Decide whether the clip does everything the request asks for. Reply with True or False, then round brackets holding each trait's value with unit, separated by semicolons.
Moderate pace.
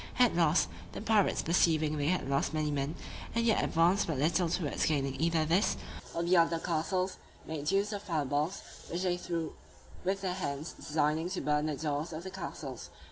True (190 wpm)